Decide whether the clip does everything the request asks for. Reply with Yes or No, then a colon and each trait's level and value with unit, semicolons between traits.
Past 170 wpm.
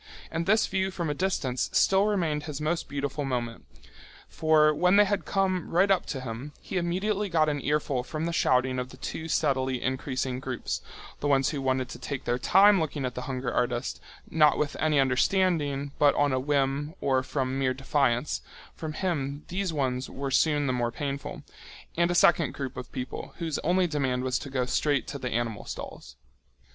Yes: average, 190 wpm